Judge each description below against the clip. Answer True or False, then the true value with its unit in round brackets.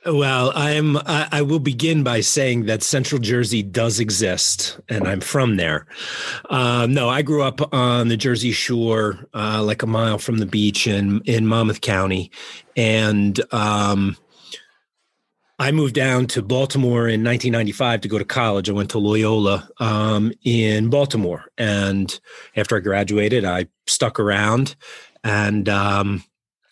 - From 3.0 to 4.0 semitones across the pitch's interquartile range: True (3.4 semitones)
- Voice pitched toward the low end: True (115 Hz)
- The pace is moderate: True (150 wpm)